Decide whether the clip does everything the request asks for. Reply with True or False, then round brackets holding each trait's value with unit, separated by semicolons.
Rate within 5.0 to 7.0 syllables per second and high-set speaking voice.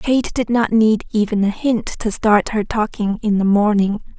False (4.4 syllables/s; 215 Hz)